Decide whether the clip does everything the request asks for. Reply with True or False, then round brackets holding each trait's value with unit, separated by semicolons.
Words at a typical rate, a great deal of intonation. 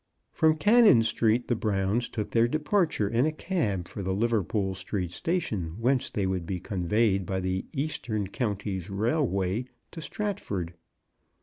True (150 wpm; 5.7 semitones)